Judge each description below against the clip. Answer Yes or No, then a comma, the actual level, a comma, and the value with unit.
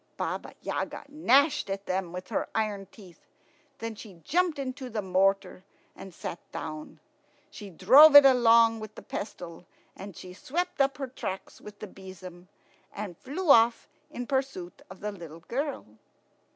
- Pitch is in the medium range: No, high, 210 Hz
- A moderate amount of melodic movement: No, wide, 6.2 semitones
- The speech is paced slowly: No, average, 150 wpm